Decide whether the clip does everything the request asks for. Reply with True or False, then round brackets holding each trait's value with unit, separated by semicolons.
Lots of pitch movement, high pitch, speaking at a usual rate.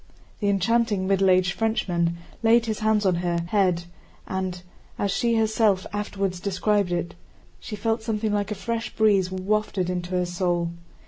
False (3.1 semitones; 200 Hz; 155 wpm)